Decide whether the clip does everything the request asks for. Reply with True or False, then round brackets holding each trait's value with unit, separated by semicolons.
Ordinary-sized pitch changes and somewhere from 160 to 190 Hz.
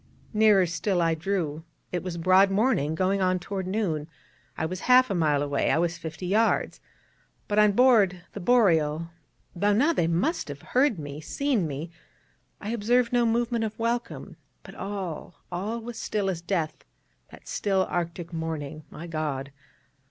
True (5.0 semitones; 185 Hz)